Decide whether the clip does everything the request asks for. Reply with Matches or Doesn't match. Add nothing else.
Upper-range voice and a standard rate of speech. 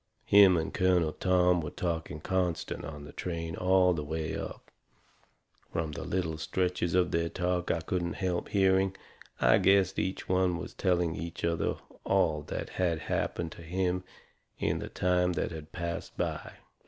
Doesn't match